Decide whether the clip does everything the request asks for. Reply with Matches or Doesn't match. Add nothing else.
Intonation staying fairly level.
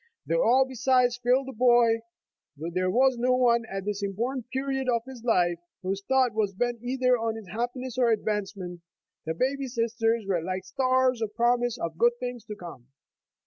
Doesn't match